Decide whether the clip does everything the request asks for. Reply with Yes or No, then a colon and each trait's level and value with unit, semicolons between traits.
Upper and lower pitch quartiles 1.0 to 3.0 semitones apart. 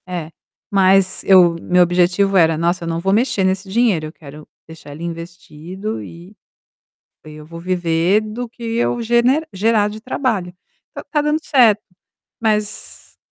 No: average, 4.4 semitones